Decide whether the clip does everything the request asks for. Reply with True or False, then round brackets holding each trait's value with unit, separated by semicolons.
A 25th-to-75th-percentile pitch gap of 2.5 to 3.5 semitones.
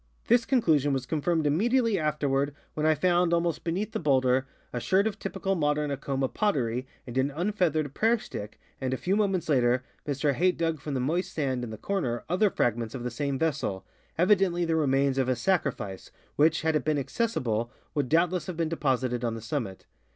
False (5.2 semitones)